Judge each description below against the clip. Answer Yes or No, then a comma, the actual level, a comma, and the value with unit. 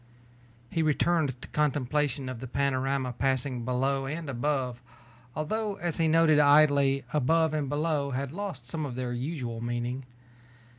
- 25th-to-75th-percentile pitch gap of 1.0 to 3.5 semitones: Yes, average, 3.2 semitones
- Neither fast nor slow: Yes, average, 145 wpm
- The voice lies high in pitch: No, medium, 140 Hz